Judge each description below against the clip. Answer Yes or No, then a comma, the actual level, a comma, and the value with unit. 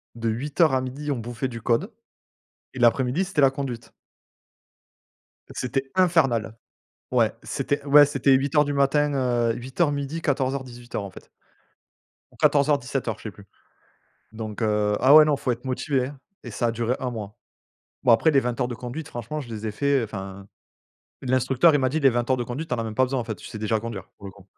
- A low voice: Yes, low, 130 Hz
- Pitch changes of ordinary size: Yes, average, 3.5 semitones